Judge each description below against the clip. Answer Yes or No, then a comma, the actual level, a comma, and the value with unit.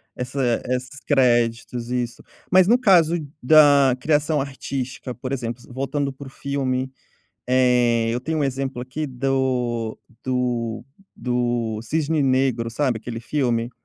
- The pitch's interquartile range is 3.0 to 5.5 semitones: No, narrow, 2.5 semitones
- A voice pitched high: No, low, 130 Hz